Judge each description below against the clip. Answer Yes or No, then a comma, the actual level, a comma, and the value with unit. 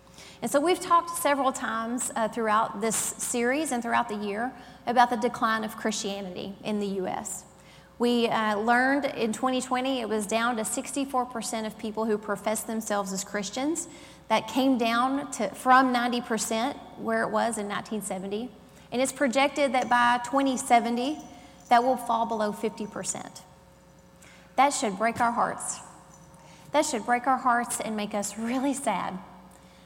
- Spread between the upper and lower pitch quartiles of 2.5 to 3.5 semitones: Yes, average, 2.9 semitones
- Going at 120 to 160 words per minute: Yes, average, 155 wpm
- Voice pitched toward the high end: Yes, high, 235 Hz